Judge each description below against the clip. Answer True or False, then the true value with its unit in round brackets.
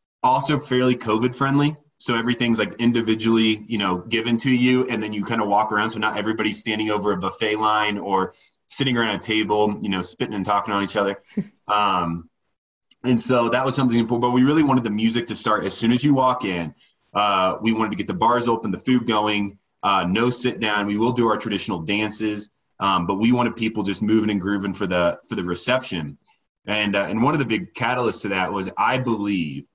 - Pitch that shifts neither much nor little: True (3.0 semitones)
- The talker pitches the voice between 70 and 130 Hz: True (110 Hz)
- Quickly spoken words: True (220 wpm)